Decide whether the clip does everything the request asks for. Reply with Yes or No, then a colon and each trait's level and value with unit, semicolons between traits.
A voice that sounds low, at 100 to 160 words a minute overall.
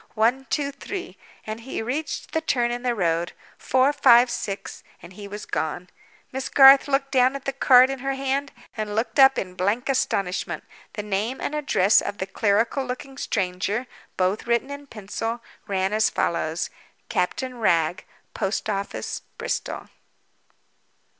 No: high, 235 Hz; average, 155 wpm